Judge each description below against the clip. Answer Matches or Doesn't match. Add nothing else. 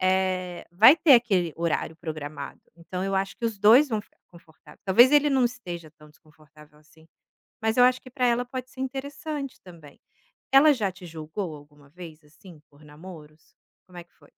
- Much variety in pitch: Matches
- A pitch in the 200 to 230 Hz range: Doesn't match